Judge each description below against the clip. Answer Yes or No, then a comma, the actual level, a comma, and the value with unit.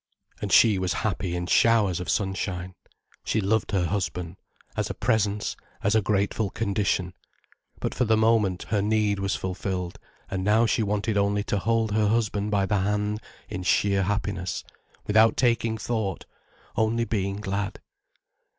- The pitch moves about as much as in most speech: No, narrow, 2.3 semitones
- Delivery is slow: No, average, 155 wpm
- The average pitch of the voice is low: Yes, low, 100 Hz